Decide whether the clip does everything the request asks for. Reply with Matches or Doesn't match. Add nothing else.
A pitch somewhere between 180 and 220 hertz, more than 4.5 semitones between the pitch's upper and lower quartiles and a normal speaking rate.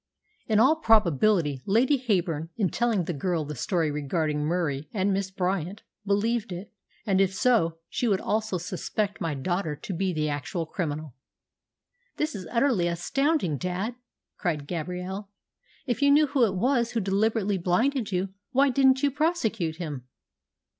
Matches